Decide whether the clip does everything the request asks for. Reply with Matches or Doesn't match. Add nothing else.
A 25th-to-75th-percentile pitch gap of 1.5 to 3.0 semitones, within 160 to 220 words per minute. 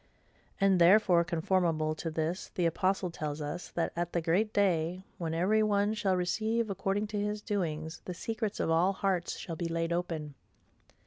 Doesn't match